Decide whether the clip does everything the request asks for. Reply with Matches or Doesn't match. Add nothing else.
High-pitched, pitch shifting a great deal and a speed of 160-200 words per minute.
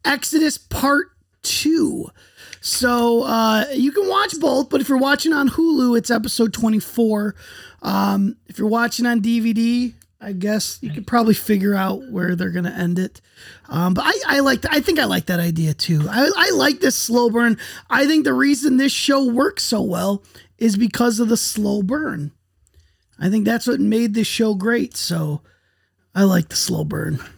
Matches